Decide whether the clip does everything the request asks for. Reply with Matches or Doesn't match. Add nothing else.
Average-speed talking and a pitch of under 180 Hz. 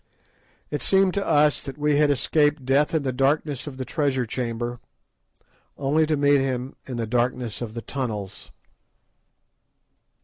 Matches